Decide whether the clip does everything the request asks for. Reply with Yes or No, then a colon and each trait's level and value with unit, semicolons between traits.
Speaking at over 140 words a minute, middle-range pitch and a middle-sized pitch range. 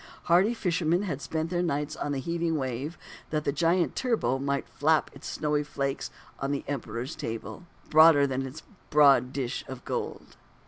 Yes: average, 170 wpm; medium, 150 Hz; average, 3.4 semitones